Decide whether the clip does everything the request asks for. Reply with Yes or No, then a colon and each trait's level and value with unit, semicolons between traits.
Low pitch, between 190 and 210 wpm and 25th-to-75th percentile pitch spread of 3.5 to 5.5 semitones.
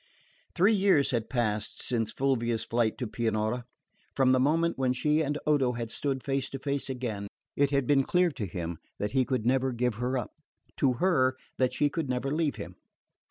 No: low, 130 Hz; average, 195 wpm; average, 3.0 semitones